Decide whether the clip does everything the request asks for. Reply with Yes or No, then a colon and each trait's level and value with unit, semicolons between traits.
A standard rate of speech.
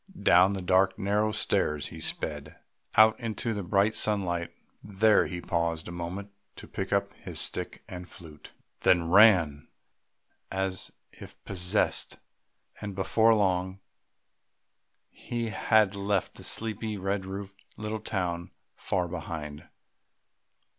No: slow, 125 wpm